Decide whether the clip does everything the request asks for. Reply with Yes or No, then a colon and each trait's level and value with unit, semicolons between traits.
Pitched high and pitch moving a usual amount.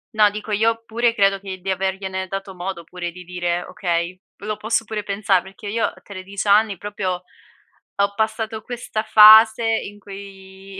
No: high, 200 Hz; narrow, 2.3 semitones